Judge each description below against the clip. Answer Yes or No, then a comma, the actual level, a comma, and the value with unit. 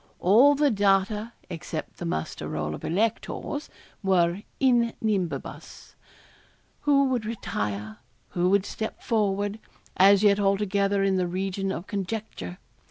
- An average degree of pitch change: Yes, average, 3.3 semitones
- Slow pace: Yes, slow, 125 wpm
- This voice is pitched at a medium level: No, high, 200 Hz